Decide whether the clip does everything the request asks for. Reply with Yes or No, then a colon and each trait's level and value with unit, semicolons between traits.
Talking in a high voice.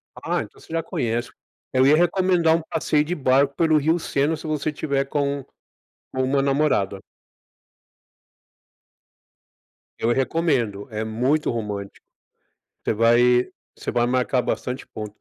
No: low, 135 Hz